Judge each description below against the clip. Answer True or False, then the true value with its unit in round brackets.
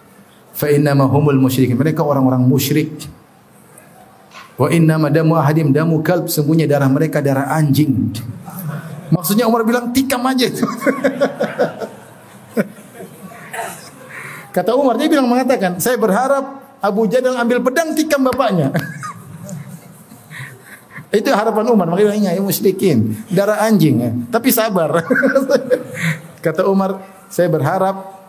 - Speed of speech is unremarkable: True (115 wpm)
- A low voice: False (190 Hz)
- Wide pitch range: True (7.8 semitones)